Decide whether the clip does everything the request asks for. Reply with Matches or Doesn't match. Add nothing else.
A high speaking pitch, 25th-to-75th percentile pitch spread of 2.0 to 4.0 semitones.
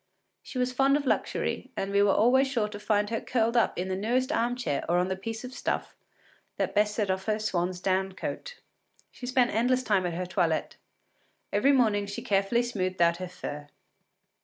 Doesn't match